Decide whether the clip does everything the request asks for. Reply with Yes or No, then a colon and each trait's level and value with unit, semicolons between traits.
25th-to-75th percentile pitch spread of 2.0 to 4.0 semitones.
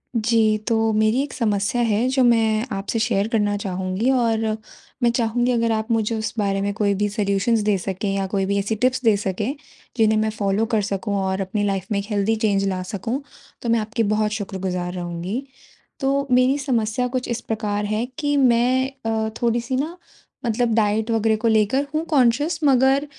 Yes: average, 3.0 semitones